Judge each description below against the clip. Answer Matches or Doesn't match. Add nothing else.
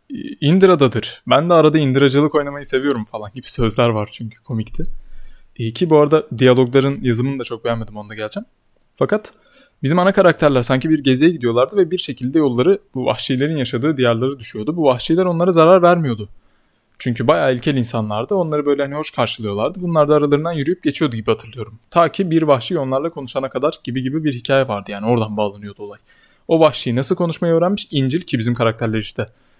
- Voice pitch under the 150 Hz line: Matches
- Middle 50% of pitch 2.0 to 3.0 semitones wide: Doesn't match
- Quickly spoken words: Matches